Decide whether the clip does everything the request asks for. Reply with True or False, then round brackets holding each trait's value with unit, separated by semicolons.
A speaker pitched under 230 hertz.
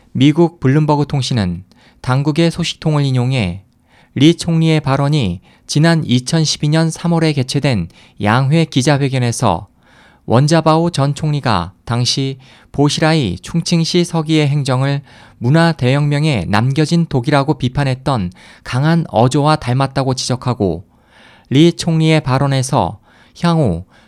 True (140 Hz)